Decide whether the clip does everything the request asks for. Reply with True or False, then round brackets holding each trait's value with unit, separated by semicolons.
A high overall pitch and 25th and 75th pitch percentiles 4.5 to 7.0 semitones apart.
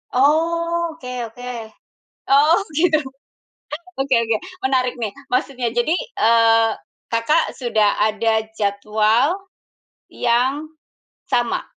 True (250 Hz; 5.1 semitones)